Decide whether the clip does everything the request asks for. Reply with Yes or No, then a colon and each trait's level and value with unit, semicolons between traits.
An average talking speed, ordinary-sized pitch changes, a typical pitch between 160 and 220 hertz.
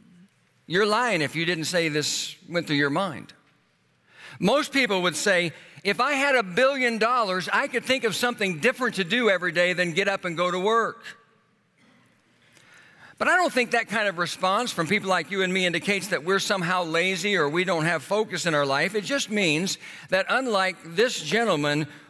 Yes: average, 195 wpm; average, 4.3 semitones; high, 190 Hz